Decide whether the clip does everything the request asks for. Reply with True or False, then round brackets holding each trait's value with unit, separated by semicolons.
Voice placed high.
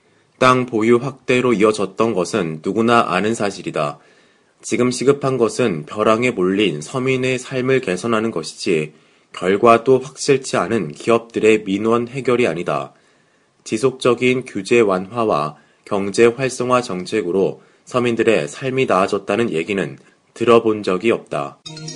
False (115 Hz)